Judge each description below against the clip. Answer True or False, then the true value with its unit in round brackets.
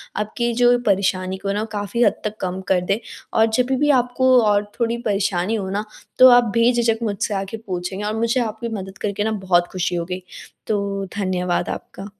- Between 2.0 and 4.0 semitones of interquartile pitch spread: True (3.3 semitones)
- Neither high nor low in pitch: False (205 Hz)